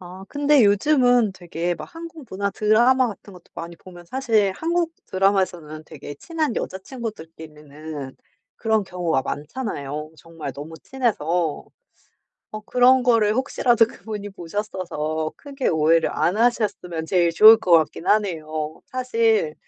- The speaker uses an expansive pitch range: Yes, wide, 7.0 semitones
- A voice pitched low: No, high, 195 Hz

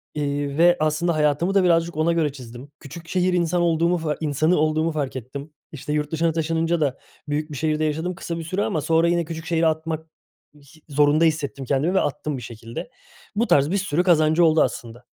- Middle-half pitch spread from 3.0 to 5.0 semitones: No, narrow, 2.4 semitones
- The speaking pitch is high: No, medium, 155 Hz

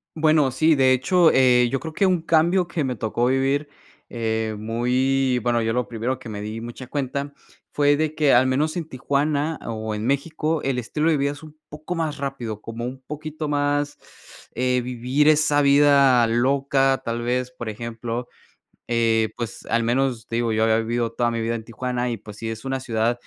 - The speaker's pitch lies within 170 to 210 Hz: No, low, 130 Hz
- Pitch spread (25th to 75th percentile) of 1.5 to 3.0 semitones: No, average, 3.8 semitones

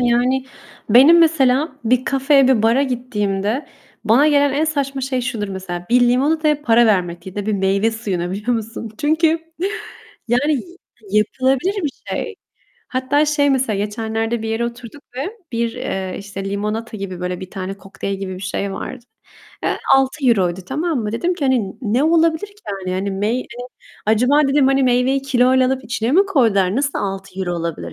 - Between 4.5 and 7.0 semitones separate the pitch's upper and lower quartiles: Yes, average, 5.2 semitones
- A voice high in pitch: Yes, high, 240 Hz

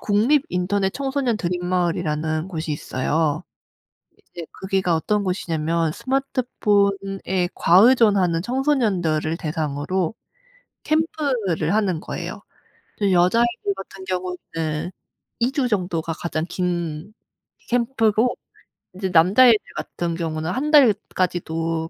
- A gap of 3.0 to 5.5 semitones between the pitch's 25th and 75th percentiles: Yes, average, 5.1 semitones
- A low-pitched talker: No, medium, 185 Hz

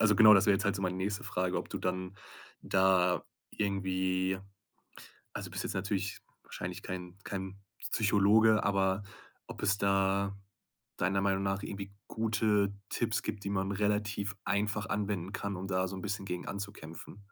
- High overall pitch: No, low, 100 Hz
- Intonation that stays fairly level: Yes, narrow, 1.6 semitones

